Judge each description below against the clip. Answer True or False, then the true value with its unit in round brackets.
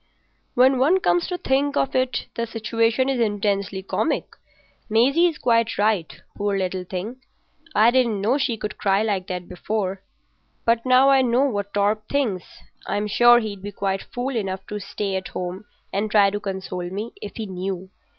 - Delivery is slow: False (170 wpm)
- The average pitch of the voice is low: False (210 Hz)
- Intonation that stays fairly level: False (3.9 semitones)